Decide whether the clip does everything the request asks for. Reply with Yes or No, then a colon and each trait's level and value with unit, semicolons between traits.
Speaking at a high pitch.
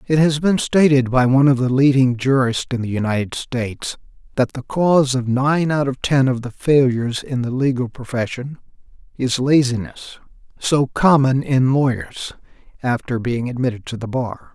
No: low, 130 Hz